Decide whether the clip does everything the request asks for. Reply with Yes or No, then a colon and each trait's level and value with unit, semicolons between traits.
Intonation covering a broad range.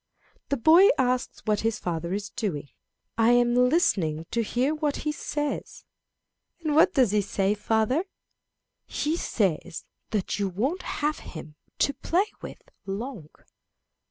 Yes: wide, 6.7 semitones